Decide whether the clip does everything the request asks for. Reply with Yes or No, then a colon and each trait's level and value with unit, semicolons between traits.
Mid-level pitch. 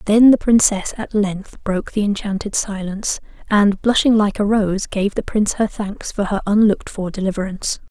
No: high, 205 Hz